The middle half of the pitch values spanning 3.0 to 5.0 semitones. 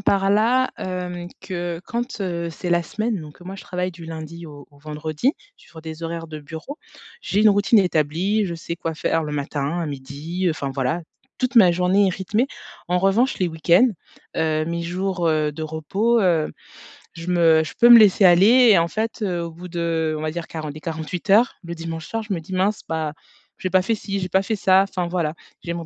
Yes: average, 3.4 semitones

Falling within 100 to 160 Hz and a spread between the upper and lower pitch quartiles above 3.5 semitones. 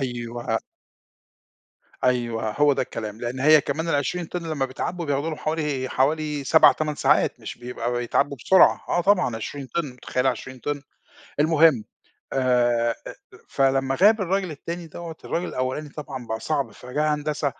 Yes: medium, 140 Hz; average, 3.9 semitones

